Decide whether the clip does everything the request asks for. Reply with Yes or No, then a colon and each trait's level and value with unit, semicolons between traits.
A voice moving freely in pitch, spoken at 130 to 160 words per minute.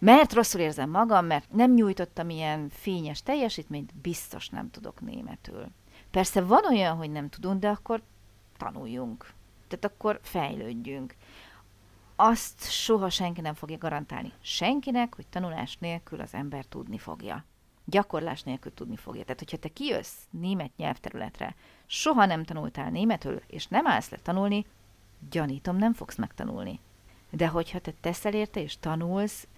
Yes: wide, 6.1 semitones; average, 140 wpm